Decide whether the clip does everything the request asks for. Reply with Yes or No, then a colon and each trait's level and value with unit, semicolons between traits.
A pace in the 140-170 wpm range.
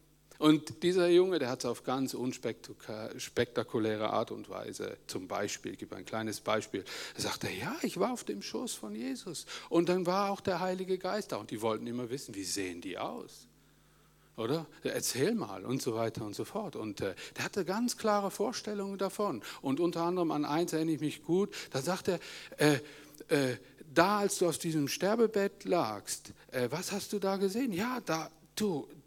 No: fast, 190 wpm